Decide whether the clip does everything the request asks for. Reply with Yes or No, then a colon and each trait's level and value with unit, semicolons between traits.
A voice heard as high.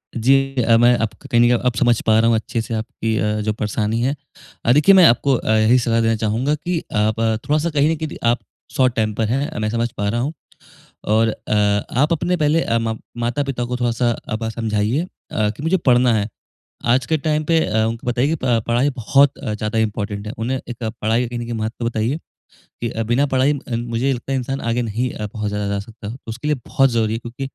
No: low, 120 Hz